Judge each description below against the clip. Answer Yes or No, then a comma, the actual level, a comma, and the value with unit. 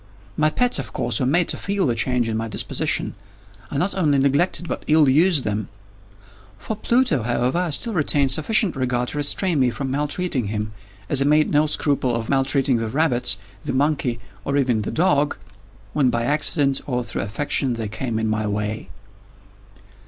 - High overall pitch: No, low, 135 Hz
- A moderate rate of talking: Yes, average, 180 wpm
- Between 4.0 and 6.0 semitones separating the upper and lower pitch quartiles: Yes, average, 4.4 semitones